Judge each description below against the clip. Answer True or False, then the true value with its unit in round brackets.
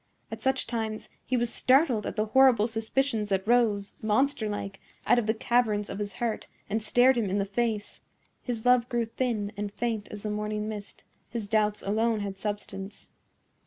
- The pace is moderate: True (185 wpm)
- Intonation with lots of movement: False (2.4 semitones)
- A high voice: True (220 Hz)